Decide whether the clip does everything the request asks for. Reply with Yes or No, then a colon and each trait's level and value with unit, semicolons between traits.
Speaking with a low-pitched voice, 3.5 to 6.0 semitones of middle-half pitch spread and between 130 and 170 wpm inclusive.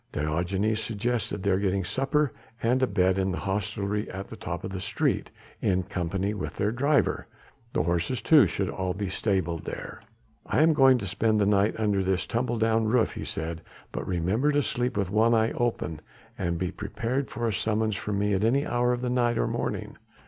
No: low, 105 Hz; average, 4.0 semitones; average, 200 wpm